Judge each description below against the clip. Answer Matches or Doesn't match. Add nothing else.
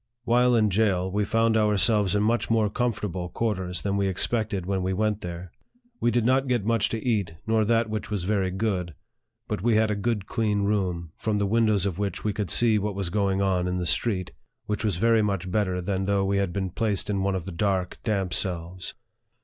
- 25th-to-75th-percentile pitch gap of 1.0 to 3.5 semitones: Matches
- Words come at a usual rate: Doesn't match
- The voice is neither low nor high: Doesn't match